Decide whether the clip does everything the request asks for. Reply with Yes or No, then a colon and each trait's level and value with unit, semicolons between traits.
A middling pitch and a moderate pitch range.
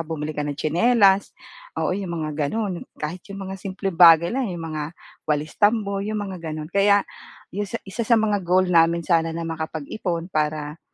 Yes: medium, 175 Hz; average, 4.1 semitones